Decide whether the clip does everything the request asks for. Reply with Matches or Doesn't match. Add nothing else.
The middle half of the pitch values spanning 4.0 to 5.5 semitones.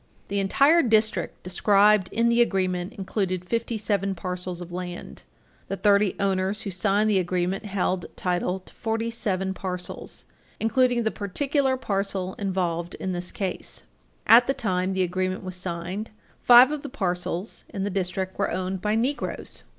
Doesn't match